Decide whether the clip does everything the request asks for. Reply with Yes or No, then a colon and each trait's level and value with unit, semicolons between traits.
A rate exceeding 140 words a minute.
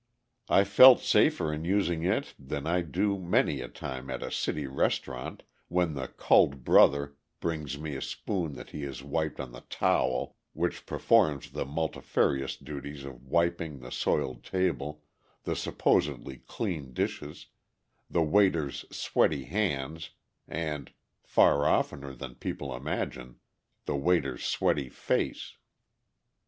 No: slow, 135 wpm